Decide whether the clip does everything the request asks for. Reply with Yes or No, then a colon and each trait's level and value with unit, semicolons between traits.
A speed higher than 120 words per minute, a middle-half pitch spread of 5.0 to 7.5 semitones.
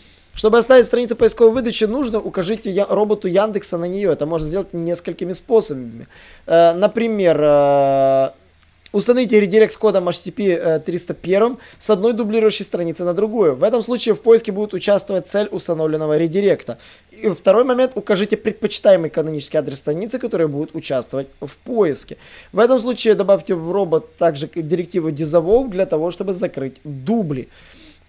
Yes: average, 145 wpm; average, 5.3 semitones